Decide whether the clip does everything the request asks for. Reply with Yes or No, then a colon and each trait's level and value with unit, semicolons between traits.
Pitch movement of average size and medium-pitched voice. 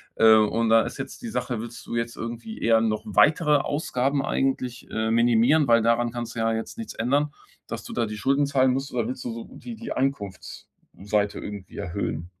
No: average, 3.4 semitones; low, 120 Hz